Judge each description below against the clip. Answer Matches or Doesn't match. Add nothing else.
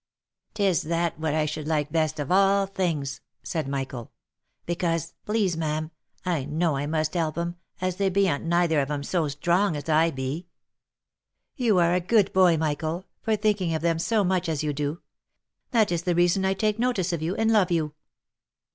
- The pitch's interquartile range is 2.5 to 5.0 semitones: Matches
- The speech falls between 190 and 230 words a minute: Matches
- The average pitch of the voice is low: Doesn't match